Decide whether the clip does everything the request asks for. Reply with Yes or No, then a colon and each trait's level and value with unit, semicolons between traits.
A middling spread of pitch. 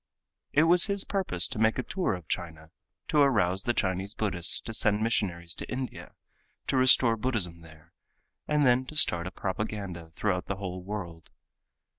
No: wide, 6.3 semitones